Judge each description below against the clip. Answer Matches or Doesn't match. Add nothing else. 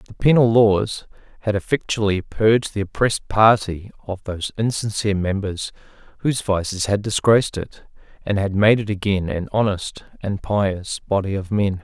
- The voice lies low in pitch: Matches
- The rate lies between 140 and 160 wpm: Matches